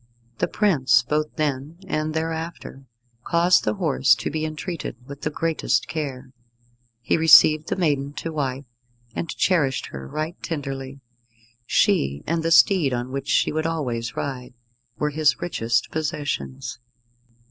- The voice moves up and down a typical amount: Yes, average, 3.7 semitones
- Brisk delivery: No, average, 140 wpm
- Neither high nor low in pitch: Yes, medium, 150 Hz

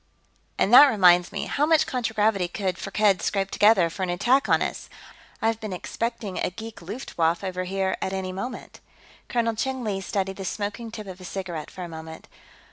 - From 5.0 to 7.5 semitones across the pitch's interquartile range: No, average, 3.6 semitones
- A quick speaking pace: No, average, 190 wpm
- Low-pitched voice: No, high, 195 Hz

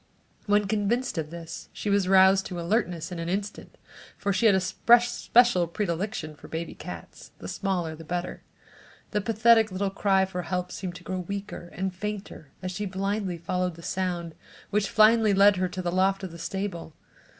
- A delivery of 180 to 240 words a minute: Yes, average, 185 wpm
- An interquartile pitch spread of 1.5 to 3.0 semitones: Yes, narrow, 2.6 semitones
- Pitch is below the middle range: No, high, 190 Hz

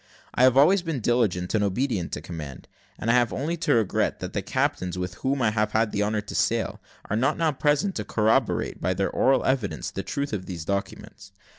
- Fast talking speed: Yes, fast, 220 wpm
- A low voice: Yes, low, 110 Hz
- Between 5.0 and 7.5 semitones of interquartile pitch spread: Yes, average, 5.3 semitones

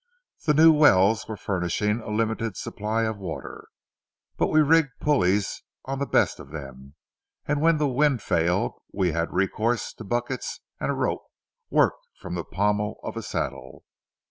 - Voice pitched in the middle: No, low, 110 Hz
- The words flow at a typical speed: Yes, average, 165 wpm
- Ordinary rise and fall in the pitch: No, wide, 6.6 semitones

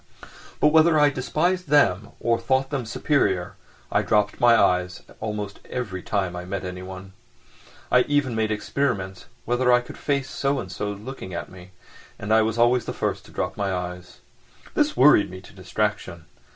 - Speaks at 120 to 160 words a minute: No, average, 175 wpm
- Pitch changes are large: Yes, wide, 5.8 semitones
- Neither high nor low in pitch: No, low, 110 Hz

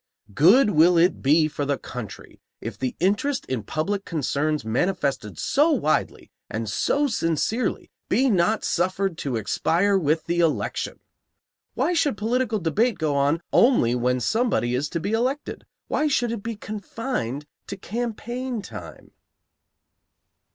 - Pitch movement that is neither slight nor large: No, wide, 8.0 semitones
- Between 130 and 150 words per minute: Yes, average, 140 wpm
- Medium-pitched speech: Yes, medium, 180 Hz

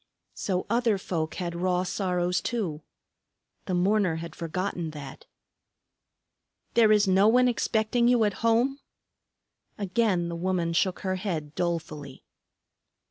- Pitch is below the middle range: No, medium, 185 Hz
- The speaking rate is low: Yes, slow, 125 wpm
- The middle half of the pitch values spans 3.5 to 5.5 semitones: Yes, average, 4.0 semitones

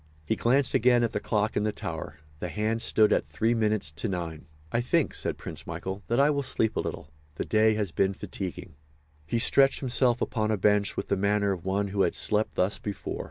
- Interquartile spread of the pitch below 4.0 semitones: Yes, average, 3.3 semitones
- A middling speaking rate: No, fast, 220 wpm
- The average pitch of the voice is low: Yes, low, 105 Hz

